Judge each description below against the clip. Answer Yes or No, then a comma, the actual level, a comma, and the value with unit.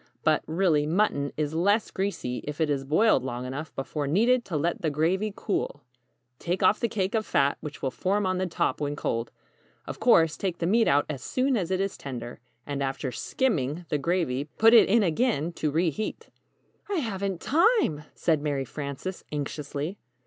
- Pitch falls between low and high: Yes, medium, 165 Hz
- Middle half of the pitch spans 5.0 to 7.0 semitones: Yes, wide, 5.6 semitones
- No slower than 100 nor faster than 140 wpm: No, average, 190 wpm